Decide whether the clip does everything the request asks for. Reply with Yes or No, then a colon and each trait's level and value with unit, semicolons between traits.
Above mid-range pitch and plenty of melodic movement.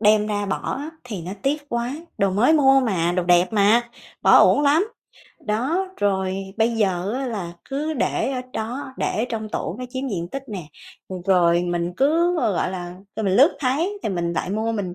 Yes: high, 220 Hz; wide, 6.3 semitones